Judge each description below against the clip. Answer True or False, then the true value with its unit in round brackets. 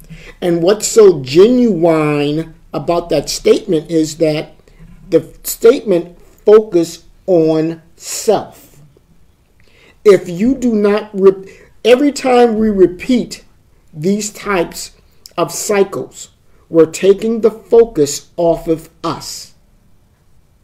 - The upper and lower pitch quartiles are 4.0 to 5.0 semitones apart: True (4.7 semitones)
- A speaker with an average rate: False (100 wpm)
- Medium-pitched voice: True (175 Hz)